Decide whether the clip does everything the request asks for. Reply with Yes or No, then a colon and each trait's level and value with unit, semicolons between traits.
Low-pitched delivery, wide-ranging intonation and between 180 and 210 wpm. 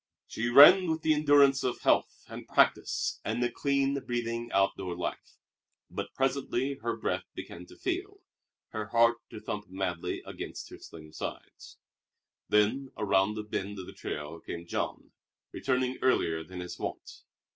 No: low, 115 Hz; wide, 6.0 semitones; average, 155 wpm